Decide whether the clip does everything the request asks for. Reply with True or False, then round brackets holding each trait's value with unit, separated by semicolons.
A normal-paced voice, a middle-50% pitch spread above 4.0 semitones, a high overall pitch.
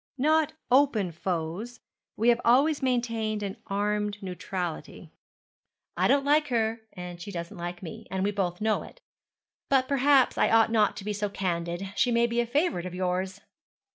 True (170 wpm; 5.0 semitones; 210 Hz)